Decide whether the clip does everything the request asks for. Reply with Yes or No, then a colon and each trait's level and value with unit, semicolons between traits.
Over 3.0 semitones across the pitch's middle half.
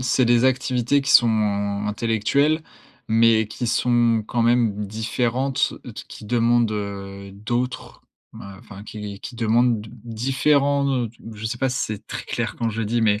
No: average, 2.7 semitones